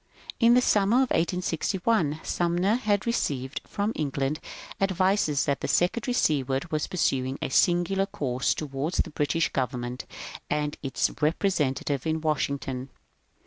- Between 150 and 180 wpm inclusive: No, slow, 135 wpm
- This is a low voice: No, medium, 155 Hz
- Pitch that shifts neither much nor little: No, wide, 5.9 semitones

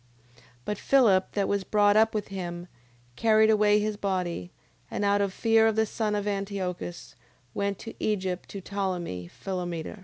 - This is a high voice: Yes, high, 200 Hz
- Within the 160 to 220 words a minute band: Yes, average, 165 wpm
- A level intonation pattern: Yes, narrow, 2.3 semitones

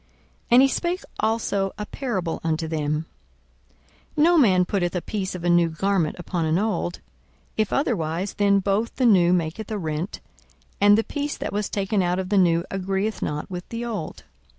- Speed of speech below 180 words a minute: No, average, 185 wpm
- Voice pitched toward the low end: No, high, 195 Hz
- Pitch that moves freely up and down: No, average, 3.9 semitones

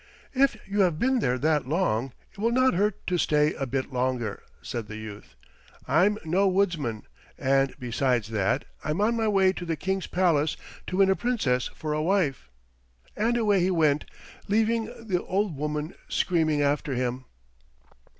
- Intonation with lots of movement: Yes, wide, 6.8 semitones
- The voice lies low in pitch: No, medium, 160 Hz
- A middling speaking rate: Yes, average, 170 wpm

